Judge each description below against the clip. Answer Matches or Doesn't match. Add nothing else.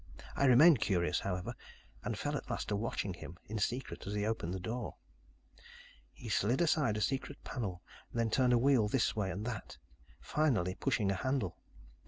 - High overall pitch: Doesn't match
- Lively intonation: Doesn't match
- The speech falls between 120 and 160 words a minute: Doesn't match